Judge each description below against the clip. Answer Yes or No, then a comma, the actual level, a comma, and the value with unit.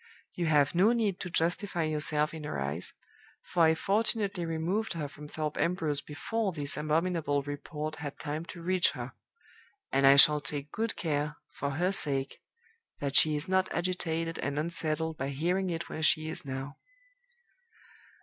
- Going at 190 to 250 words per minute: No, average, 165 wpm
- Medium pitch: Yes, medium, 160 Hz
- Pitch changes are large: No, average, 3.3 semitones